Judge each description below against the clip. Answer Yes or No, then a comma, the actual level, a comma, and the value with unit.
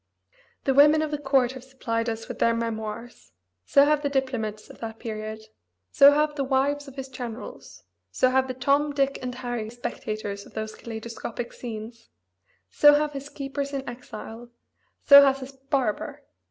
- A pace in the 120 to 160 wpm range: No, average, 170 wpm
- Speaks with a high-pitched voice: Yes, very high, 260 Hz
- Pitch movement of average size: Yes, average, 3.4 semitones